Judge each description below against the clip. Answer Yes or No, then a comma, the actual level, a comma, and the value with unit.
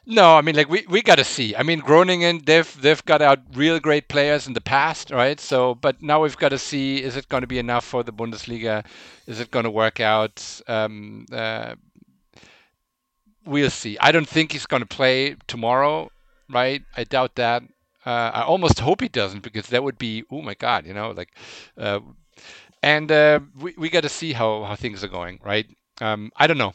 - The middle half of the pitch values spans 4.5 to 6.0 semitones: Yes, average, 4.9 semitones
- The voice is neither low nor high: No, low, 130 Hz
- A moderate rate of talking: No, fast, 215 wpm